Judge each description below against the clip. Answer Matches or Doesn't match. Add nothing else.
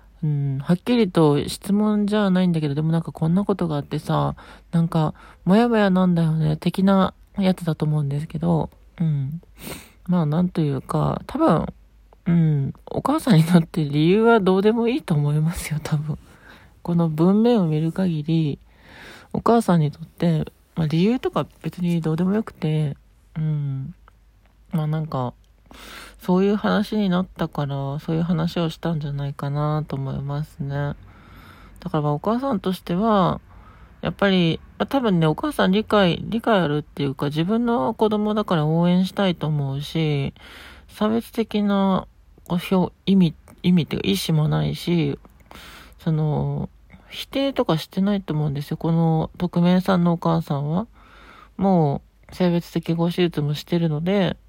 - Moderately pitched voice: Matches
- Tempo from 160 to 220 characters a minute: Doesn't match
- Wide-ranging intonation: Doesn't match